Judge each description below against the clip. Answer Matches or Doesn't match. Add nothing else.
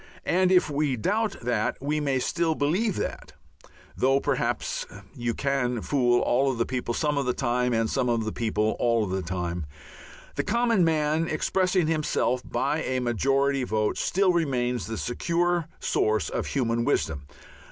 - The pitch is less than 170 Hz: Matches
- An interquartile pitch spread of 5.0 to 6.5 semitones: Matches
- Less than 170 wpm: Matches